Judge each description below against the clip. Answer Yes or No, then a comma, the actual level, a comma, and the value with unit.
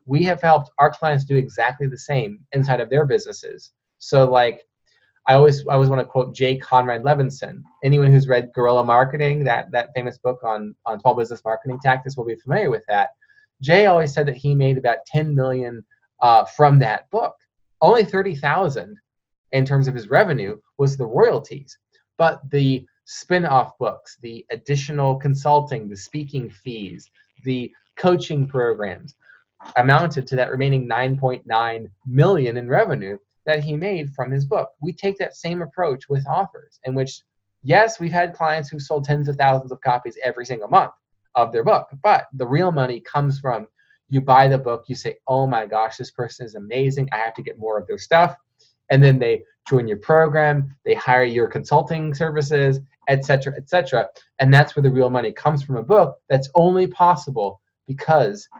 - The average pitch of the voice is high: No, low, 135 Hz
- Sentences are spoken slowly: No, average, 185 wpm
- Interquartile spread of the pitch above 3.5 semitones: No, average, 3.2 semitones